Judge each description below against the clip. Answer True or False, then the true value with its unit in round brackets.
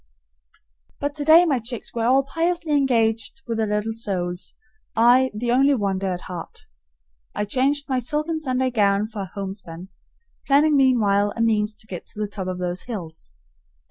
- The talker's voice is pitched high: True (225 Hz)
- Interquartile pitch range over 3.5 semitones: True (5.1 semitones)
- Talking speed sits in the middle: True (165 wpm)